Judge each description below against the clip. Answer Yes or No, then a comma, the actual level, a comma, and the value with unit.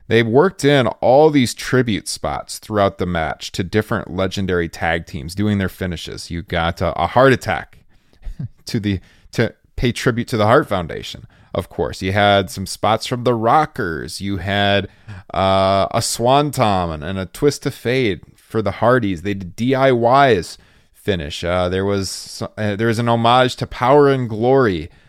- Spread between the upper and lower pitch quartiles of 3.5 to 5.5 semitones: Yes, average, 4.3 semitones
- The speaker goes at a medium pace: Yes, average, 175 wpm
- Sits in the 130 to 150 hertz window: No, low, 105 Hz